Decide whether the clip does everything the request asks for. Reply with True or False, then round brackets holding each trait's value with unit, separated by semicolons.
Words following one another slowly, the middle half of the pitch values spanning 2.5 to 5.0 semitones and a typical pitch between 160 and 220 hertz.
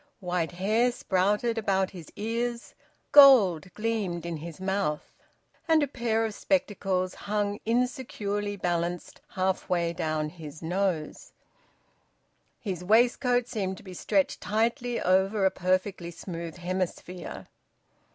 True (120 wpm; 4.0 semitones; 190 Hz)